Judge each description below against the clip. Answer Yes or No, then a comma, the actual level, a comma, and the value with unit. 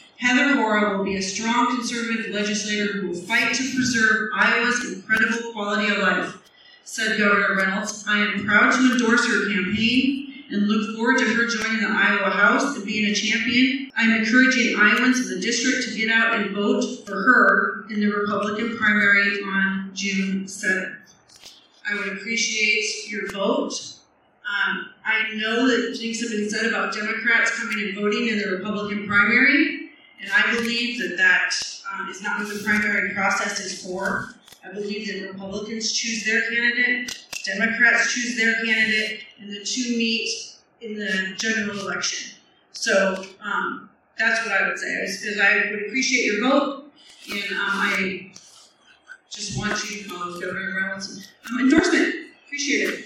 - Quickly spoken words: No, average, 160 wpm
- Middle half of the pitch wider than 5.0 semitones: No, average, 2.7 semitones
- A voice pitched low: No, high, 215 Hz